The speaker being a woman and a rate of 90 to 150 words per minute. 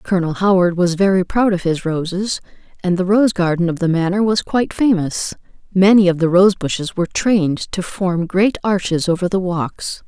No: female; average, 190 wpm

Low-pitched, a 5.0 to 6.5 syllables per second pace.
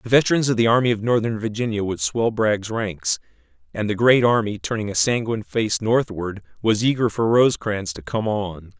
Yes: low, 110 Hz; 5.3 syllables/s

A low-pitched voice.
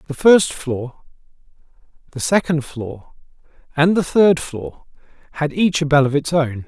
No: medium, 150 Hz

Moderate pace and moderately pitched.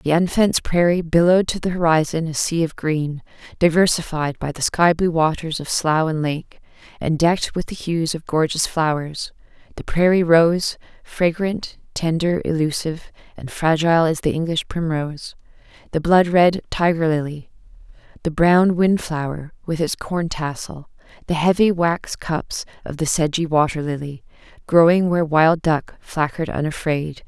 Yes: average, 145 wpm; medium, 165 Hz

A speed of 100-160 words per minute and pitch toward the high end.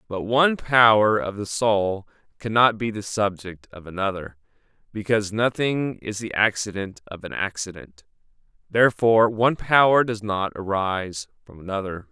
No: average, 140 wpm; low, 105 Hz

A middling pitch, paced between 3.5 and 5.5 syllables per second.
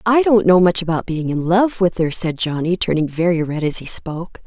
Yes: medium, 175 Hz; 5.3 syllables/s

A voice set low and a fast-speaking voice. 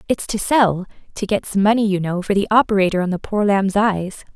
No: high, 200 Hz; fast, 220 wpm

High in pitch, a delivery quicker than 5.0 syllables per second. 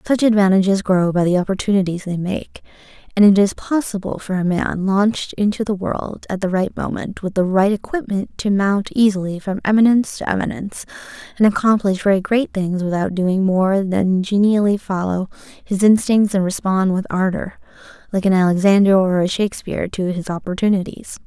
Yes: high, 195 Hz; 5.3 syllables/s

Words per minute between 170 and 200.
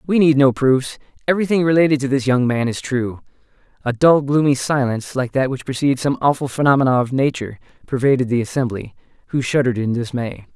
Yes: average, 180 wpm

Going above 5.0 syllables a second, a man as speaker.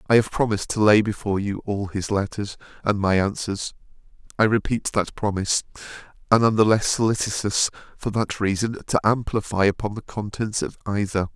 Yes: 5.5 syllables/s; male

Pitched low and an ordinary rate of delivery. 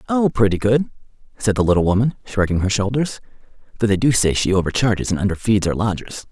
Yes: low, 105 Hz; average, 190 wpm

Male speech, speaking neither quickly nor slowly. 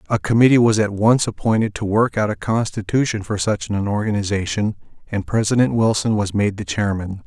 Yes: male; average, 180 wpm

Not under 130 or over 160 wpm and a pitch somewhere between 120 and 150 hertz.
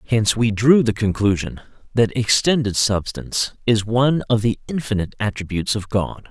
No: average, 150 wpm; low, 110 Hz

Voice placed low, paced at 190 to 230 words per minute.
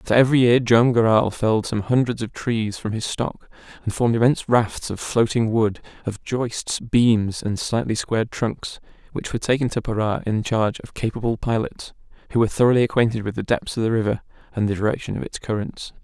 Yes: low, 115 Hz; average, 200 wpm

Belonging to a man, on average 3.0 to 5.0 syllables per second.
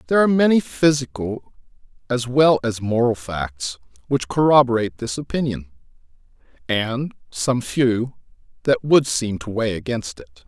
Yes: male; 4.7 syllables/s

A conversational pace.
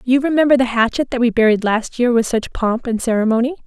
No: fast, 230 wpm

